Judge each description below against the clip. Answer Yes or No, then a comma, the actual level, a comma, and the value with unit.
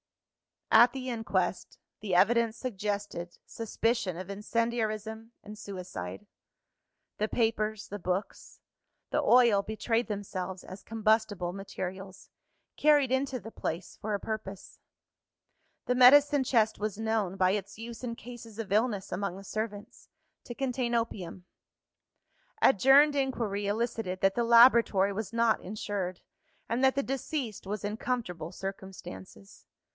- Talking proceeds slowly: Yes, slow, 130 wpm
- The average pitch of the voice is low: No, high, 215 Hz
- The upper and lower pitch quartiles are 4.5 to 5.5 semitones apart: No, average, 3.4 semitones